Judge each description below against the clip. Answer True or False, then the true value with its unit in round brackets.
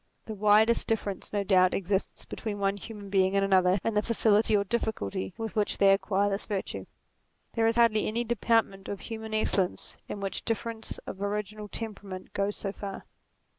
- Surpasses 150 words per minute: True (175 wpm)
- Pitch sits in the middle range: False (205 Hz)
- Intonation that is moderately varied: False (2.0 semitones)